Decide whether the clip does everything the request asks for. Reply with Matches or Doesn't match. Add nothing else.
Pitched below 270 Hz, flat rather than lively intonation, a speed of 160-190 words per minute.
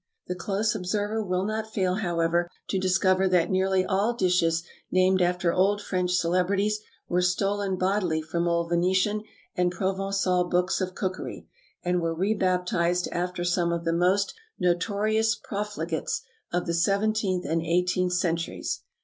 Doesn't match